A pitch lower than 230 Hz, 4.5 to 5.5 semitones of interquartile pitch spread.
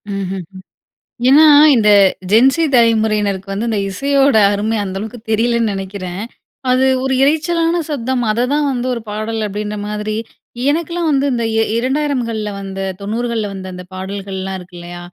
Yes: high, 220 Hz; average, 4.9 semitones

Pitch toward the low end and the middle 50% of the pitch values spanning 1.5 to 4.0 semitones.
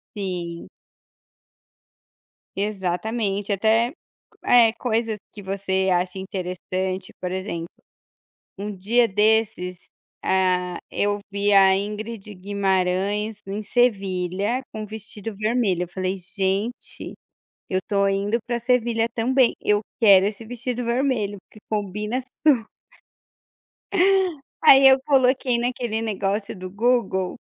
No: high, 205 Hz; average, 3.3 semitones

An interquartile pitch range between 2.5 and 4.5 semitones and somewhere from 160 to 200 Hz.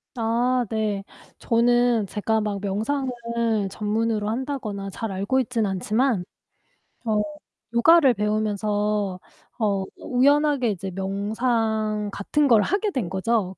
No: average, 3.2 semitones; high, 220 Hz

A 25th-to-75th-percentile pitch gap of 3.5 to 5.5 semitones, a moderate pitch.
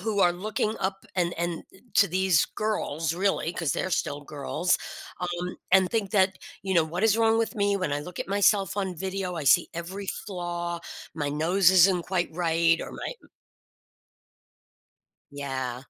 No: average, 2.7 semitones; medium, 180 Hz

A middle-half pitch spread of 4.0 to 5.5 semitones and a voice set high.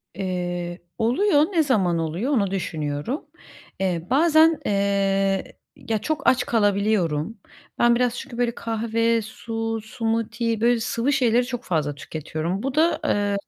Yes: average, 4.4 semitones; high, 225 Hz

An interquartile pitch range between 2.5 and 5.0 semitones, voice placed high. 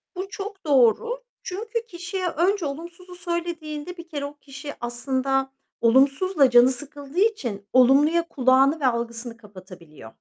No: wide, 5.6 semitones; very high, 290 Hz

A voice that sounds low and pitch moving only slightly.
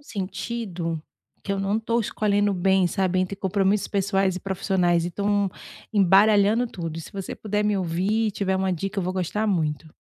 No: high, 195 Hz; narrow, 2.1 semitones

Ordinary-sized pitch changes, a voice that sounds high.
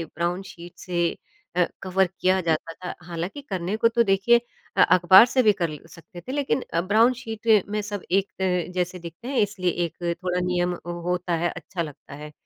No: average, 3.0 semitones; medium, 180 Hz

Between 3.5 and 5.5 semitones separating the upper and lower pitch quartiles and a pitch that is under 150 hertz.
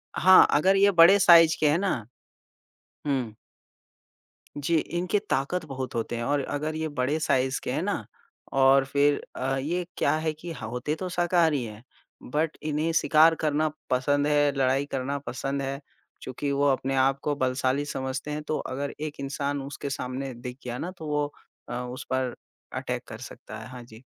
No: average, 3.1 semitones; medium, 140 Hz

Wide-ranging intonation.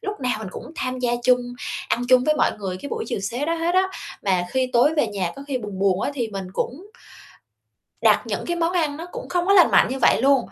Yes: wide, 7.4 semitones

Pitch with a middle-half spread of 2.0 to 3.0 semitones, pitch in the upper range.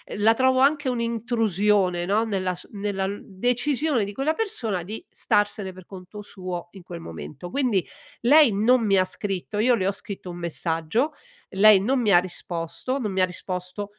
No: average, 4.3 semitones; high, 205 Hz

